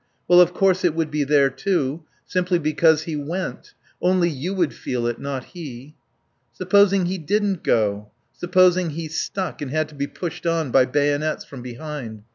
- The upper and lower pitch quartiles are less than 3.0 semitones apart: No, average, 4.3 semitones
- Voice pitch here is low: No, medium, 155 Hz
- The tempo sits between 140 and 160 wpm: No, average, 175 wpm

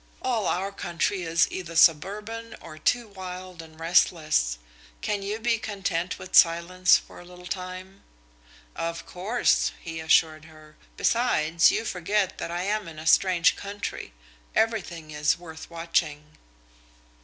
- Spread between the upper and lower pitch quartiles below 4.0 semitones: Yes, average, 3.3 semitones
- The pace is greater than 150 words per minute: No, average, 140 wpm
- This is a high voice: No, medium, 180 Hz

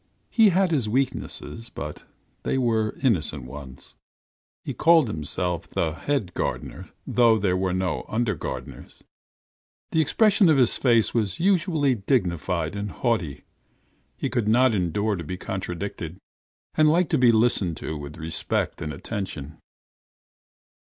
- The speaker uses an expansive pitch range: Yes, wide, 7.3 semitones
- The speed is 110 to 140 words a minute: Yes, slow, 135 wpm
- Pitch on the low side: Yes, low, 105 Hz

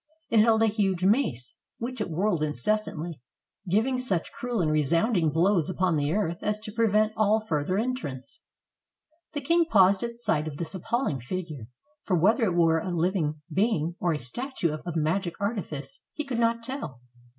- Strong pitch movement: Yes, wide, 6.0 semitones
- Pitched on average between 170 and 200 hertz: Yes, high, 190 Hz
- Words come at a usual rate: Yes, average, 175 wpm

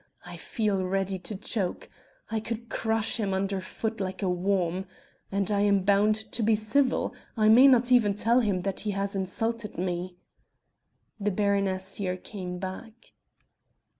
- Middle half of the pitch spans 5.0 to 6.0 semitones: No, average, 2.8 semitones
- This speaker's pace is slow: No, average, 160 wpm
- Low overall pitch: No, high, 200 Hz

